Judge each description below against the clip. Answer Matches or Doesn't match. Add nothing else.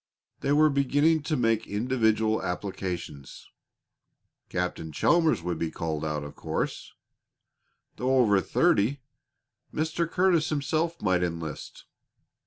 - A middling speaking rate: Doesn't match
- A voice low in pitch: Matches